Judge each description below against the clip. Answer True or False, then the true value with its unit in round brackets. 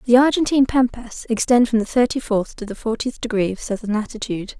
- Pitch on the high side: True (230 Hz)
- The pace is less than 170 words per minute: False (195 wpm)